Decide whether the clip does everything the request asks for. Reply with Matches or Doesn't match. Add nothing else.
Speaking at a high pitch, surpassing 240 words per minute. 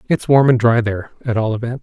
Doesn't match